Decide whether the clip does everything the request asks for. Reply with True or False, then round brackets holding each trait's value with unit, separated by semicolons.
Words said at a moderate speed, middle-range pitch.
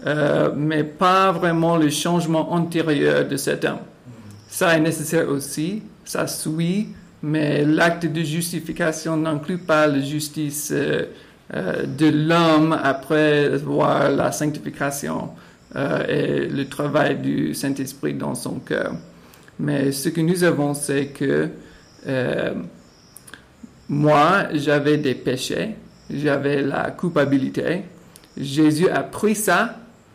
False (115 wpm; 155 Hz)